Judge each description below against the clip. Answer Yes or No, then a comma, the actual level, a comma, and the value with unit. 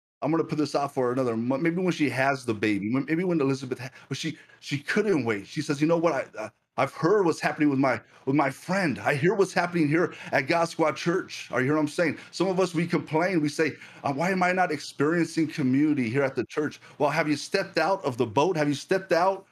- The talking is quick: Yes, fast, 255 wpm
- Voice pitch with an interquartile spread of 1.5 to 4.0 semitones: Yes, average, 3.5 semitones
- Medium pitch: Yes, medium, 155 Hz